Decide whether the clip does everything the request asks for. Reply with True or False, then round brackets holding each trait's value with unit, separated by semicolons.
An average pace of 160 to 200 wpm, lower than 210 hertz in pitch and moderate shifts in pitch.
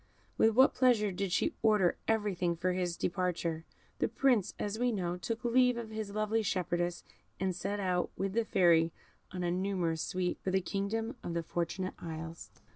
True (180 wpm; 190 Hz; 3.8 semitones)